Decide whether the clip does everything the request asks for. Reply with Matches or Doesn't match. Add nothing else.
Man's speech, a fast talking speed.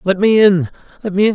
Matches